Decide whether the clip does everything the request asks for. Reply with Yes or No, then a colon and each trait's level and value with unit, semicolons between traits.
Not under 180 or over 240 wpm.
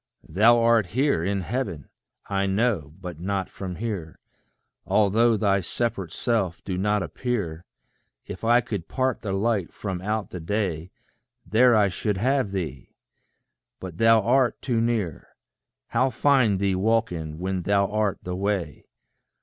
No: average, 145 wpm